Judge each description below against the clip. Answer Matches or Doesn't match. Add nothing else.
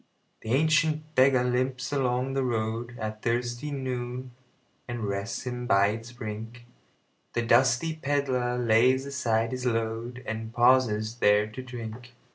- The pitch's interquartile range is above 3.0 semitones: Doesn't match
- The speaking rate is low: Matches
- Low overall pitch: Matches